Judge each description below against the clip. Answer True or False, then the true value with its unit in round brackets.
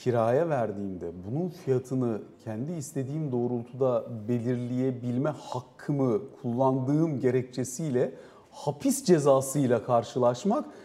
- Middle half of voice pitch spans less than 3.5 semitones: True (2.6 semitones)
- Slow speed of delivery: True (75 wpm)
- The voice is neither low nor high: False (130 Hz)